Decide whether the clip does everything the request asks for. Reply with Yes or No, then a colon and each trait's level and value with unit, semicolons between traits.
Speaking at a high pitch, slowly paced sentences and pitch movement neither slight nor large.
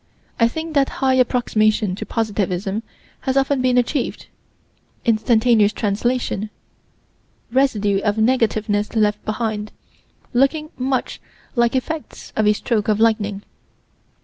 Yes: high, 225 Hz; slow, 115 wpm; average, 3.4 semitones